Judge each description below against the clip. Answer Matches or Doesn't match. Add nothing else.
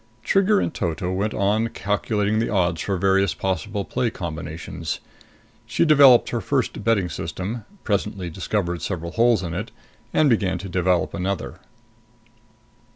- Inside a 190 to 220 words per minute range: Doesn't match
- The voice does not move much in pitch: Doesn't match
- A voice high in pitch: Doesn't match